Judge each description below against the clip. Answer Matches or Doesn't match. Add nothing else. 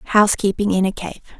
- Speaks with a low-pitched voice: Doesn't match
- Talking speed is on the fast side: Doesn't match